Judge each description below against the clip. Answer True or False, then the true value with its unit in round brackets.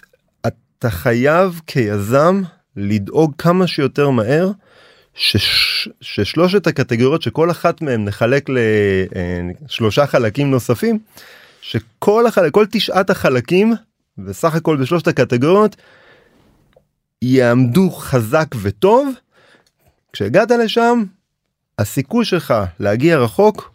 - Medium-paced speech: False (90 wpm)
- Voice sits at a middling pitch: True (155 Hz)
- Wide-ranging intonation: True (8.2 semitones)